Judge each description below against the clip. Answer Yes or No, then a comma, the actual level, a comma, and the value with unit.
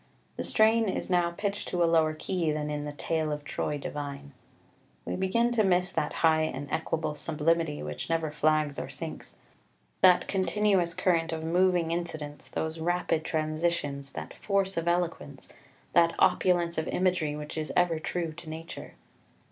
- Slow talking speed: No, average, 165 wpm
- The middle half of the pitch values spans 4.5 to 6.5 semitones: No, narrow, 2.6 semitones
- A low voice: No, medium, 165 Hz